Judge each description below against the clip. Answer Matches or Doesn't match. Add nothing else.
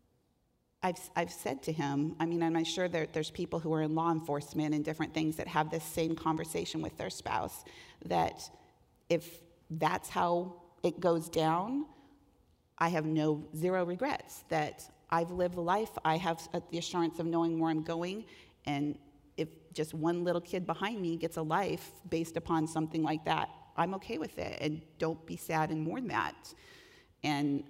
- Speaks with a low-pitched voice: Doesn't match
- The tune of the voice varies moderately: Doesn't match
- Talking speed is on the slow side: Doesn't match